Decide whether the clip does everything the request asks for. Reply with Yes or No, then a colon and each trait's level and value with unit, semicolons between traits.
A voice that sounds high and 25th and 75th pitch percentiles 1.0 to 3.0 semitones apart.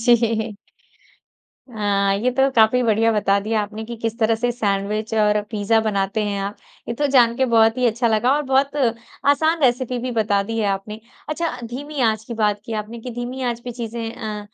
Yes: high, 225 Hz; narrow, 2.6 semitones